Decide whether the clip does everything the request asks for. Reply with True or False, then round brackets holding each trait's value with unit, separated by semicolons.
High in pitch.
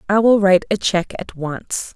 True (195 Hz)